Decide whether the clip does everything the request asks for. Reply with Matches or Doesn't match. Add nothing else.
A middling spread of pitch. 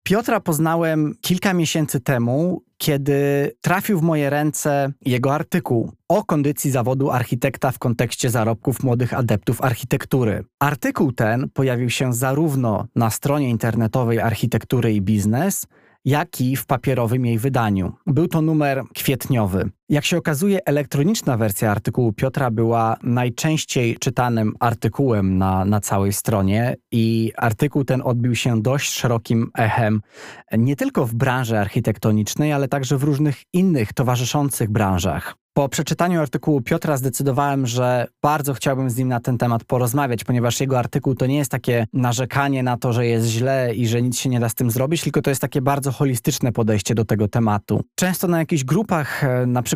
Matches